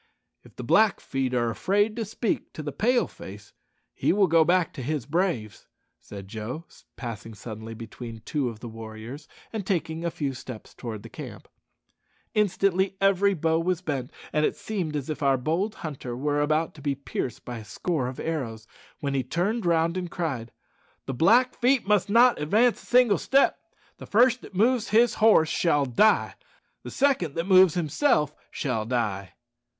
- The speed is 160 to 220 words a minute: Yes, average, 175 wpm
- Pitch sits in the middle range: Yes, medium, 155 Hz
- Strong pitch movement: Yes, wide, 7.9 semitones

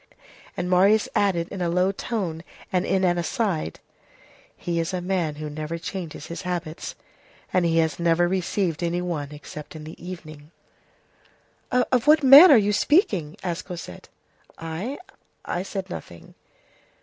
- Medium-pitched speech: Yes, medium, 175 Hz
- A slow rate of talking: No, average, 150 wpm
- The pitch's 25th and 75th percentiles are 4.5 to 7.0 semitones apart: No, average, 3.1 semitones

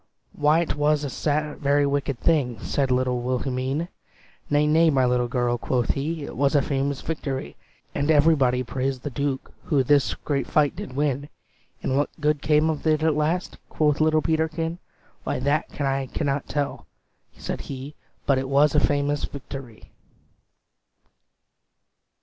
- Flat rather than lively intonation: Yes, narrow, 2.3 semitones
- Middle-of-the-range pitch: Yes, medium, 145 Hz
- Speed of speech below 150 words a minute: No, average, 155 wpm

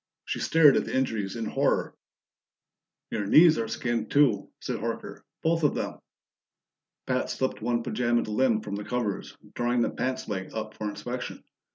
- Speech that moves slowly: No, average, 165 wpm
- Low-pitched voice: Yes, low, 120 Hz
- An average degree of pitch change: Yes, average, 3.3 semitones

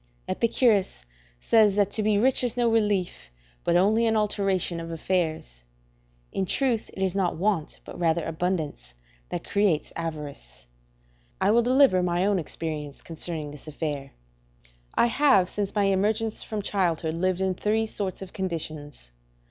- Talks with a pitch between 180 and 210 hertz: Yes, medium, 185 Hz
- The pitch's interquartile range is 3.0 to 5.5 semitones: Yes, average, 4.5 semitones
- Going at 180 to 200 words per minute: No, average, 150 wpm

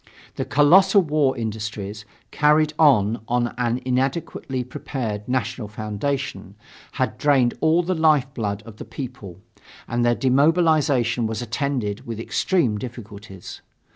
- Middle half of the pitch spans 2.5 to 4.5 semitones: No, average, 5.1 semitones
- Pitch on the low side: Yes, low, 125 Hz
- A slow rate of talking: Yes, slow, 120 wpm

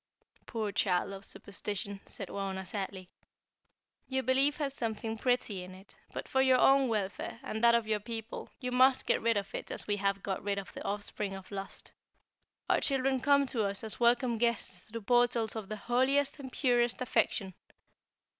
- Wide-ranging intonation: No, average, 4.1 semitones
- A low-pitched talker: No, high, 225 Hz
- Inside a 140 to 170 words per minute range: No, average, 185 wpm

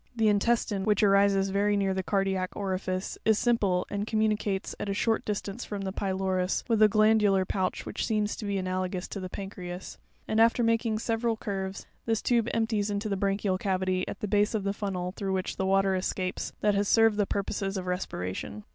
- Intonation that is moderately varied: No, narrow, 2.1 semitones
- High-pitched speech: Yes, high, 200 Hz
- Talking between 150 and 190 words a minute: No, average, 200 wpm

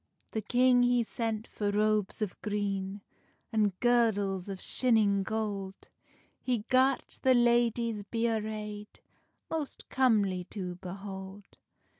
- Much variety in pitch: No, average, 3.0 semitones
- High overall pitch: Yes, high, 215 Hz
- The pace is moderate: No, slow, 115 wpm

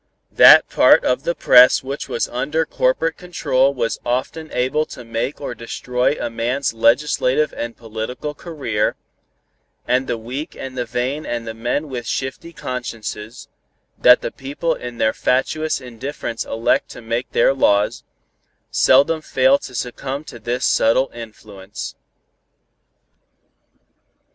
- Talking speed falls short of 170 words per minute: Yes, slow, 135 wpm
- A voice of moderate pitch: No, low, 125 Hz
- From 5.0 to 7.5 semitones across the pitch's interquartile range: No, average, 3.2 semitones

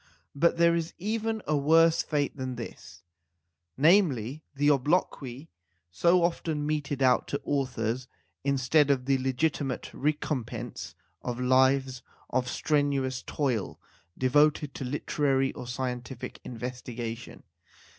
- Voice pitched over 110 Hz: Yes, low, 135 Hz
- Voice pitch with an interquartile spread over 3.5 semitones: No, average, 3.2 semitones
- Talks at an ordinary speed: No, slow, 115 wpm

